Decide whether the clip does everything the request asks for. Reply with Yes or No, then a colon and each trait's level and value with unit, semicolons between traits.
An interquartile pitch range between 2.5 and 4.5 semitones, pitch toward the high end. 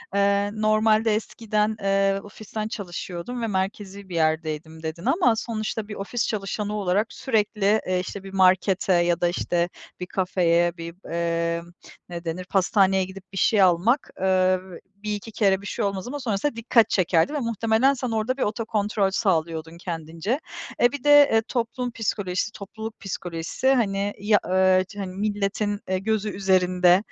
Yes: average, 3.1 semitones; high, 195 Hz